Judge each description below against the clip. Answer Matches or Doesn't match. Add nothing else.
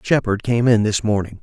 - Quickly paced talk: Matches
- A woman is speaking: Doesn't match